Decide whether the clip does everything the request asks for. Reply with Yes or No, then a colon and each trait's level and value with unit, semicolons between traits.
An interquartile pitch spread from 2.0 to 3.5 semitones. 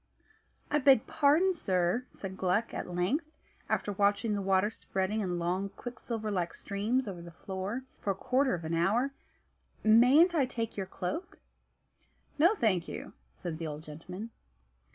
No: wide, 5.5 semitones